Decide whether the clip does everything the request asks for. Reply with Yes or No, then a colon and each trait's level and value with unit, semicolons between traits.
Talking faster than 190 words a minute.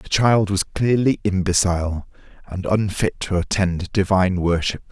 No: slow, 135 wpm